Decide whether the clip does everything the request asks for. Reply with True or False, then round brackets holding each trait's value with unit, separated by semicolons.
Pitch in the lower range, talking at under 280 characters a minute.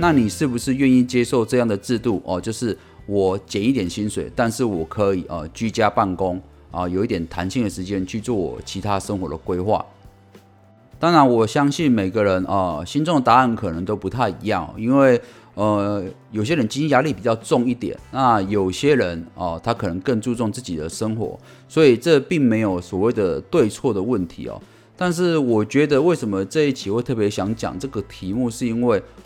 False (105 Hz; 295 characters per minute)